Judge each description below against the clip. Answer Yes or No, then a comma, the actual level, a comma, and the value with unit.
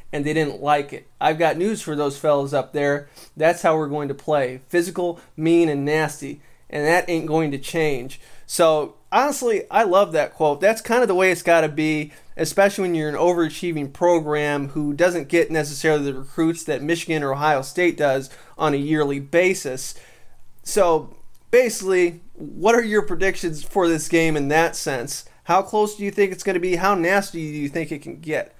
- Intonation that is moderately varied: Yes, average, 3.2 semitones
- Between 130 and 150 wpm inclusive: No, average, 200 wpm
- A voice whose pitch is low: No, medium, 160 Hz